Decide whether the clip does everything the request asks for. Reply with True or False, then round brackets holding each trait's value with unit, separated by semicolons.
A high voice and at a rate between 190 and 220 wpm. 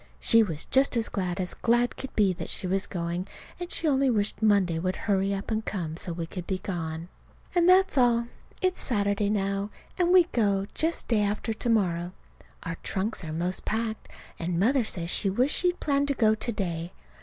True (205 Hz; 200 wpm)